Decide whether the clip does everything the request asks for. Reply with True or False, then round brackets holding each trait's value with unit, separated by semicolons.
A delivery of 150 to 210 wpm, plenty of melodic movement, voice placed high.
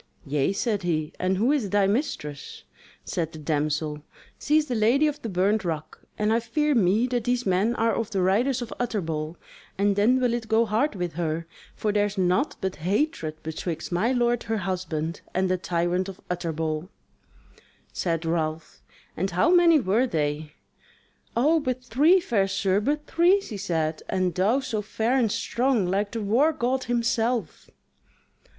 True (175 wpm; 5.9 semitones; 205 Hz)